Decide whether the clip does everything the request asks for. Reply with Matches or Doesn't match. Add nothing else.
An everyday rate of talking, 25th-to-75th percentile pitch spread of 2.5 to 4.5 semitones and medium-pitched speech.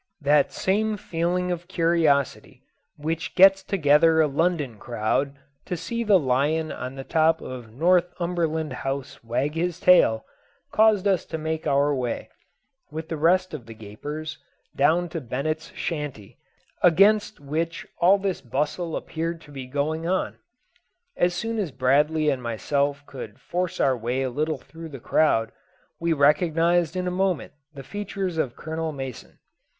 Matches